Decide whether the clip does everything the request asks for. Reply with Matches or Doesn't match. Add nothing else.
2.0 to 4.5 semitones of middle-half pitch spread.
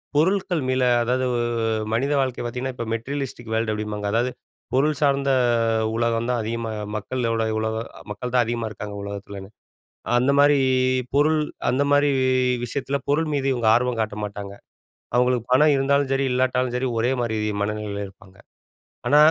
Matches